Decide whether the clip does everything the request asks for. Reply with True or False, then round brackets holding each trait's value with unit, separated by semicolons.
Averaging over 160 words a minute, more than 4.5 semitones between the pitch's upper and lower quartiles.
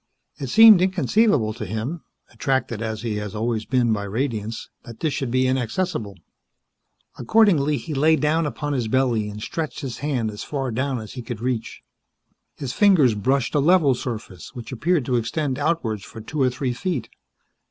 True (175 wpm; 5.0 semitones)